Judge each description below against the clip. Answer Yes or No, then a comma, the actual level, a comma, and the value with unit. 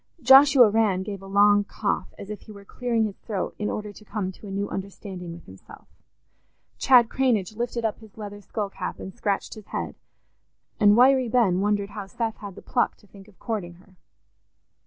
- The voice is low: No, high, 205 Hz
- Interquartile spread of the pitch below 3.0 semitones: Yes, narrow, 2.5 semitones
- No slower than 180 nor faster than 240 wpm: Yes, average, 200 wpm